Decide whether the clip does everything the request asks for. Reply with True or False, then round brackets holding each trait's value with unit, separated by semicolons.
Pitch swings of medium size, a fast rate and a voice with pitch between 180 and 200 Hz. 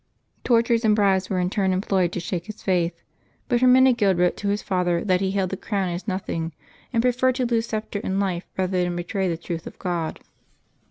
True (3.4 semitones; 210 wpm; 190 Hz)